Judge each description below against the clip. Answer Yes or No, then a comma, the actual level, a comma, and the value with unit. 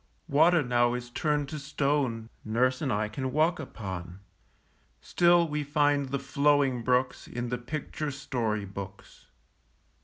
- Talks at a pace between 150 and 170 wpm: No, slow, 135 wpm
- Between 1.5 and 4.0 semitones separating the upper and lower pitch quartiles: Yes, average, 3.6 semitones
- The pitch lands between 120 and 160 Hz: Yes, low, 135 Hz